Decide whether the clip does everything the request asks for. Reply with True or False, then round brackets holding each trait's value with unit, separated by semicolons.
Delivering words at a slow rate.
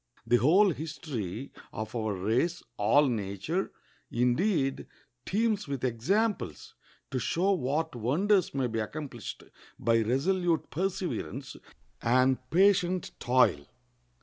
True (105 wpm)